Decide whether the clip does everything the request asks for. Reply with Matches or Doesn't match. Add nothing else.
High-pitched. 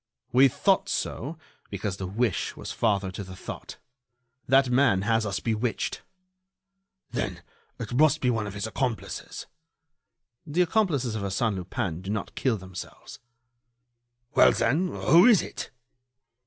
Doesn't match